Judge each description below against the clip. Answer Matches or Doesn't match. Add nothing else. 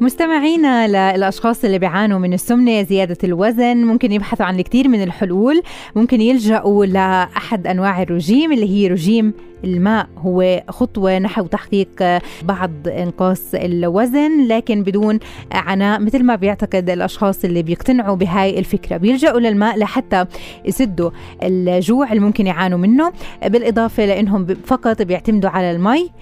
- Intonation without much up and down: Doesn't match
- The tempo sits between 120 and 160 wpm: Matches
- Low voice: Doesn't match